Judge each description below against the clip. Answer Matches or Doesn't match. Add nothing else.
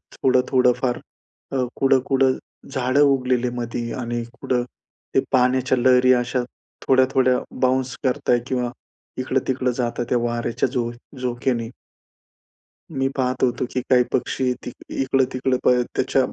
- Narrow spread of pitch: Matches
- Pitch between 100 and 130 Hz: Matches